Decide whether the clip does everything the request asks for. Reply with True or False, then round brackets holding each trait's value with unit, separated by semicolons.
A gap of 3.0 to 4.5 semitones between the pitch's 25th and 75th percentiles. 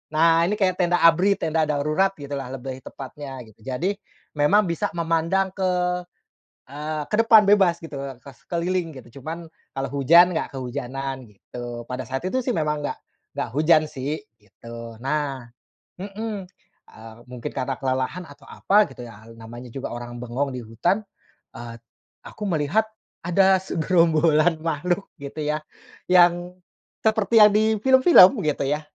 False (5.5 semitones)